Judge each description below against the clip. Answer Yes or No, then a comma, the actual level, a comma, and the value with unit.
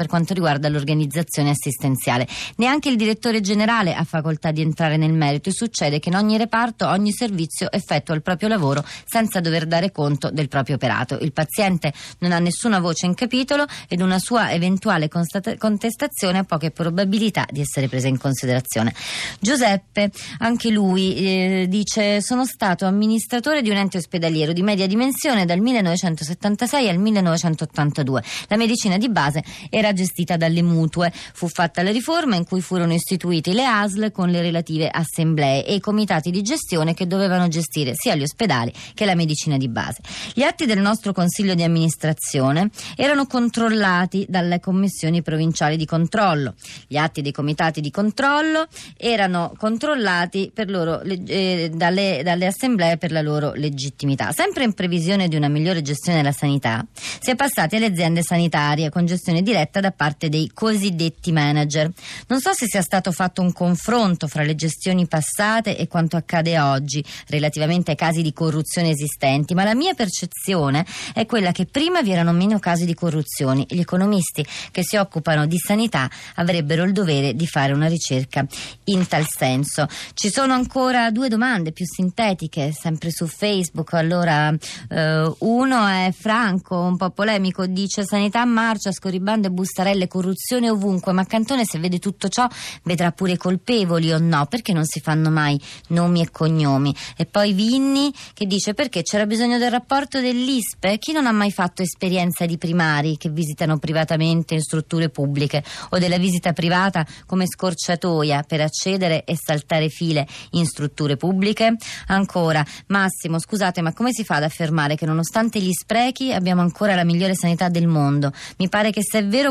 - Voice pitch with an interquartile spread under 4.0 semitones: No, average, 4.6 semitones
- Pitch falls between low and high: Yes, medium, 175 Hz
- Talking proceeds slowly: No, average, 165 wpm